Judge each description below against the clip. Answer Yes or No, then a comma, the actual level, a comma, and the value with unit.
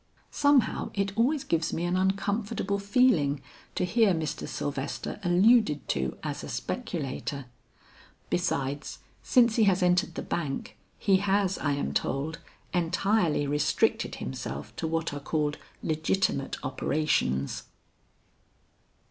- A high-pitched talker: No, medium, 175 Hz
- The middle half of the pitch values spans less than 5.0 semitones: No, wide, 5.6 semitones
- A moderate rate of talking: No, slow, 120 wpm